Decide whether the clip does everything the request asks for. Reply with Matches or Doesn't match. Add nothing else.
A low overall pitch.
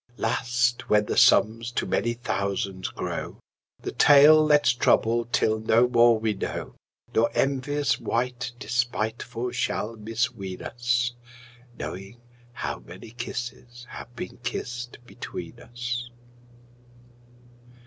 Matches